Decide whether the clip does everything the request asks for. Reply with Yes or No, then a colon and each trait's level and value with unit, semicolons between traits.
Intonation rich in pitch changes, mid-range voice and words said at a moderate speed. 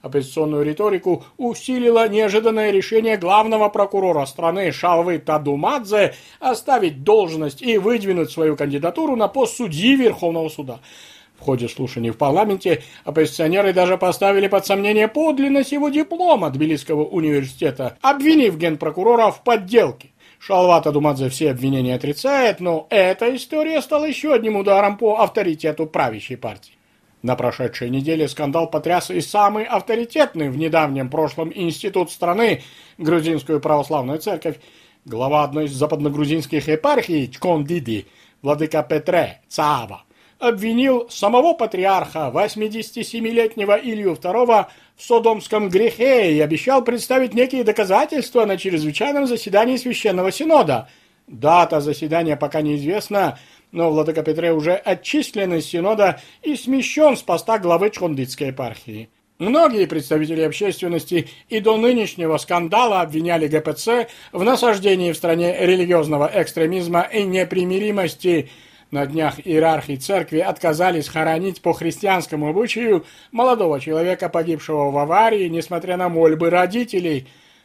Yes: wide, 6.0 semitones; medium, 180 Hz; average, 120 wpm